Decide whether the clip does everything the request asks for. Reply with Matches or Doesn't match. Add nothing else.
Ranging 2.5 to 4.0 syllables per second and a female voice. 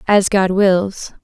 Matches